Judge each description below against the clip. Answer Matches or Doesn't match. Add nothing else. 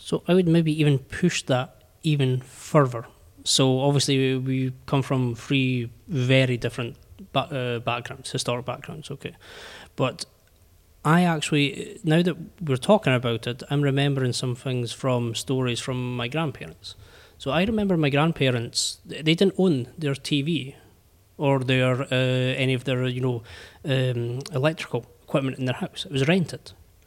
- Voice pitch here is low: Matches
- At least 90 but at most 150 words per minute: Matches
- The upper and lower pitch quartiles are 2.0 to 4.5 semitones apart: Matches